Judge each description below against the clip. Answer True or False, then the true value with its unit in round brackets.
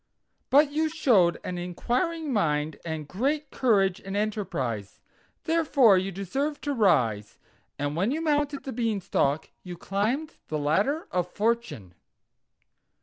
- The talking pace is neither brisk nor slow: False (130 wpm)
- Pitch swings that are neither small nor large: False (8.6 semitones)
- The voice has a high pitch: True (205 Hz)